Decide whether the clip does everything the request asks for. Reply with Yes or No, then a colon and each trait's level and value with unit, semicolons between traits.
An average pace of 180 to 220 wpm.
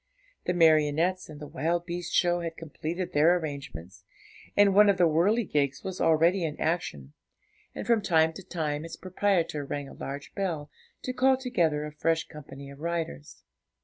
No: average, 170 wpm